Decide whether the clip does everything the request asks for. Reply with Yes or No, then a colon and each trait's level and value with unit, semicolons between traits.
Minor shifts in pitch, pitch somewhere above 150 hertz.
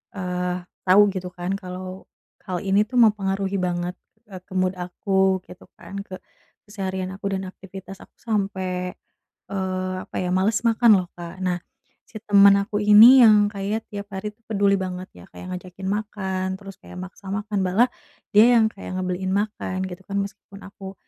Yes: narrow, 1.8 semitones; high, 190 Hz